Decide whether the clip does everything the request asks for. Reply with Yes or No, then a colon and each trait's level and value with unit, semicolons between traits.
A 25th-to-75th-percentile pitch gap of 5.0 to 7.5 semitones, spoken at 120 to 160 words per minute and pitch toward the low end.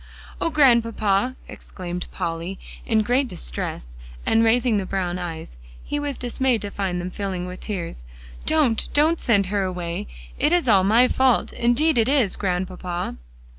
No: wide, 5.4 semitones; average, 155 wpm; high, 205 Hz